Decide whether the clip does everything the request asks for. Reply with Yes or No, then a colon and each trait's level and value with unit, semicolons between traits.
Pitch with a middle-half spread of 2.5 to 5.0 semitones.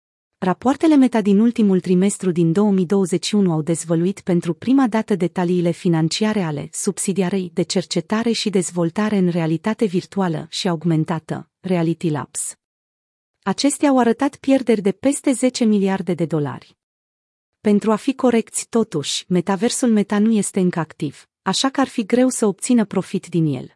Yes: average, 4.6 semitones